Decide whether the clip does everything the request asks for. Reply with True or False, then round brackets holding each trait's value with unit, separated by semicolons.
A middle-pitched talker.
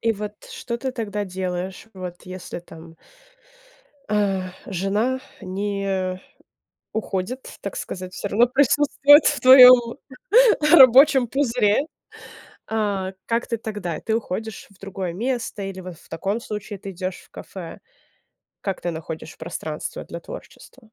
False (200 Hz)